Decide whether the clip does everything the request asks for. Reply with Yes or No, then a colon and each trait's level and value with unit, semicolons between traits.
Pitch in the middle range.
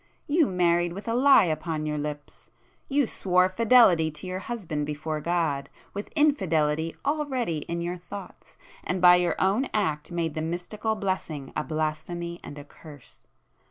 Yes: medium, 175 Hz